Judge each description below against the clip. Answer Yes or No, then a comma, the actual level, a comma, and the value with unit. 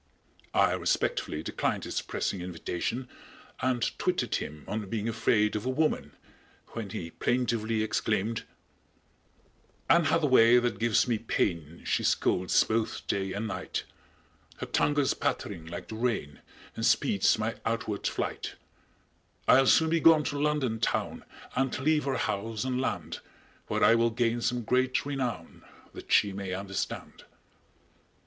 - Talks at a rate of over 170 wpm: No, average, 145 wpm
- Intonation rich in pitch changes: No, average, 4.2 semitones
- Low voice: Yes, low, 115 Hz